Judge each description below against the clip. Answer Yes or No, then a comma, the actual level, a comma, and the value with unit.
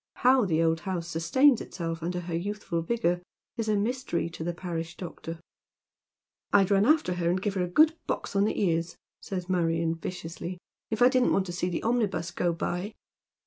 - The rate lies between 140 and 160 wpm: No, average, 200 wpm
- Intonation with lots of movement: No, average, 3.7 semitones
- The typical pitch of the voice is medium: Yes, medium, 180 Hz